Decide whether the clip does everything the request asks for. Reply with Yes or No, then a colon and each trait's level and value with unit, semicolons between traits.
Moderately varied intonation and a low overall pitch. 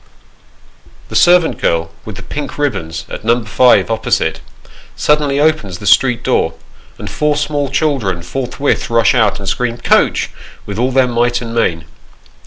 No: wide, 5.7 semitones; low, 120 Hz